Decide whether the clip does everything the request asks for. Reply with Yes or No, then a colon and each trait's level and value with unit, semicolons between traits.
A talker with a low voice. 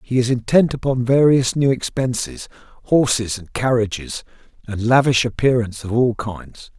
Yes: low, 120 Hz